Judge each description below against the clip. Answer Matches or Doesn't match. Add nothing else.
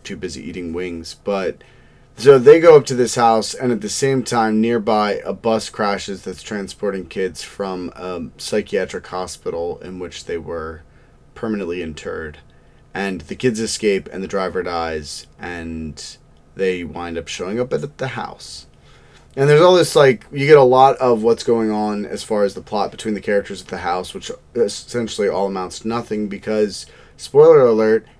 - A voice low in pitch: Matches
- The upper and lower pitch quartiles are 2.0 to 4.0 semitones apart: Doesn't match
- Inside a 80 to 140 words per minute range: Doesn't match